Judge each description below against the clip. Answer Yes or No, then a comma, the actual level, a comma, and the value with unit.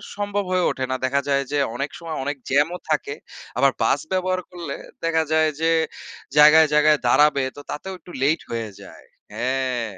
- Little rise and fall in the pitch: No, average, 3.6 semitones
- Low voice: No, medium, 150 Hz